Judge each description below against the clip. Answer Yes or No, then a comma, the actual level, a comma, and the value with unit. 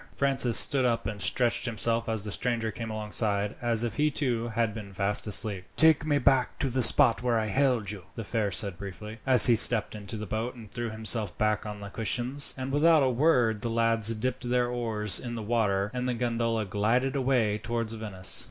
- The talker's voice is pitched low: Yes, low, 115 Hz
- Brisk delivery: Yes, fast, 210 wpm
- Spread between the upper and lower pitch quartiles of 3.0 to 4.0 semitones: No, narrow, 2.6 semitones